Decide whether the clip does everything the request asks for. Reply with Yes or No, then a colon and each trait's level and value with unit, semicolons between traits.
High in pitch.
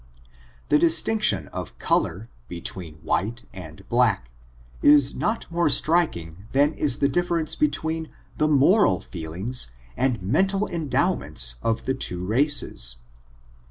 No: low, 130 Hz